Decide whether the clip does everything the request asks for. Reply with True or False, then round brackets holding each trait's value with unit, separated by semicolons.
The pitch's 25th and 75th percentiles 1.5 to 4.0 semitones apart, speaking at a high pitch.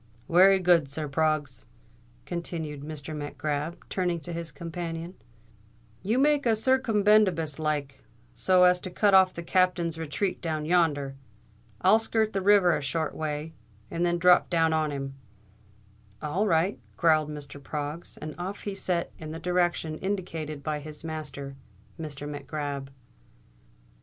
False (3.3 semitones; 165 Hz)